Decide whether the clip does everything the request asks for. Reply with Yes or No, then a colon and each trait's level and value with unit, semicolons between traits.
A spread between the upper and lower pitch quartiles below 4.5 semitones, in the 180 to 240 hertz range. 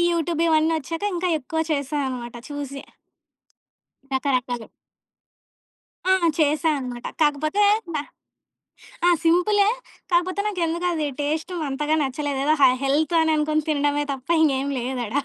No: average, 3.3 semitones; very high, 300 Hz